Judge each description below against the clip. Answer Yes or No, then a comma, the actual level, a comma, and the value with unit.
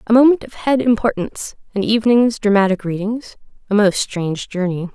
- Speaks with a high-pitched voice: Yes, high, 215 Hz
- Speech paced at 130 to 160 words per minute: Yes, slow, 135 wpm